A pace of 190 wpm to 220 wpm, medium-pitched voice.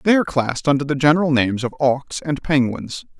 Yes: fast, 205 wpm; medium, 145 Hz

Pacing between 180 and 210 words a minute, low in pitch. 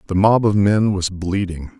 Yes: average, 200 wpm; very low, 95 Hz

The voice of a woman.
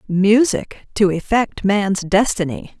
Yes: female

